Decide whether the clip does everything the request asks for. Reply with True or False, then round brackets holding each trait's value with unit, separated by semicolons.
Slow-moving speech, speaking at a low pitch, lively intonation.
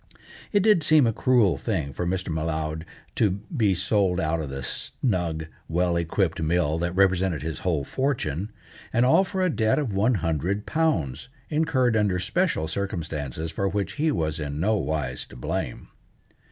False (165 wpm; 90 Hz; 6.2 semitones)